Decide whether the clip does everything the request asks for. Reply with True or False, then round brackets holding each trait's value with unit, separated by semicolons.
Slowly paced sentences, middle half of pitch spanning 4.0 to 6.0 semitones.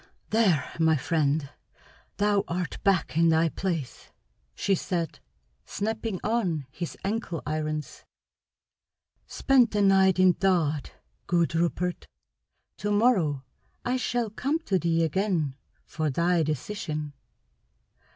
True (110 wpm; 4.6 semitones)